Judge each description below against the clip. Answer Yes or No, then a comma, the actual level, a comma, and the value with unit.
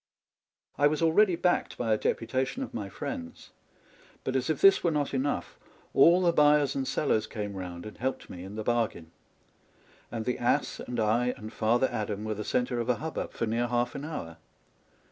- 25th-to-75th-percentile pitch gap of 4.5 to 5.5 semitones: Yes, average, 5.1 semitones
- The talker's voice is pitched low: Yes, low, 120 Hz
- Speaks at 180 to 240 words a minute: Yes, average, 195 wpm